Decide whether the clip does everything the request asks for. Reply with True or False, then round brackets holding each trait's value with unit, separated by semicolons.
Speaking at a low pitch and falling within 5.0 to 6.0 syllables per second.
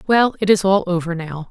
False (185 Hz; 5.3 syllables/s)